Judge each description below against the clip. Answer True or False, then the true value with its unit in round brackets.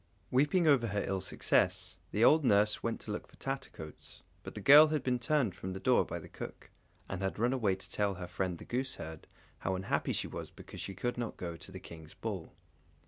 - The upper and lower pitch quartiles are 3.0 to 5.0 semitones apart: False (5.4 semitones)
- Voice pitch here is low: True (105 Hz)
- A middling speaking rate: False (220 wpm)